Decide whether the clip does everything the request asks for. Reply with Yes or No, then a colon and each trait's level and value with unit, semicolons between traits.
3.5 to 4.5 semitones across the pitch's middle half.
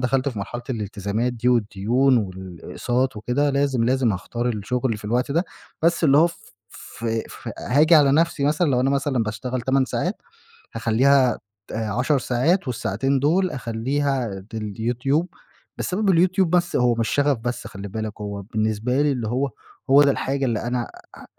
Yes: average, 4.0 semitones